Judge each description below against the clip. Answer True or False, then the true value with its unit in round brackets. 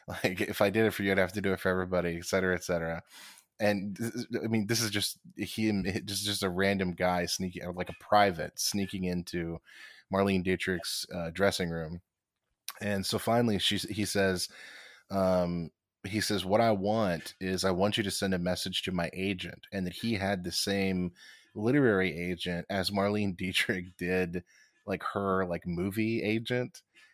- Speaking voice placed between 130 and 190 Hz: False (95 Hz)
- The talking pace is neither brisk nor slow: True (180 wpm)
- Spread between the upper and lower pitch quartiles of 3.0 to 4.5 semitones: False (2.4 semitones)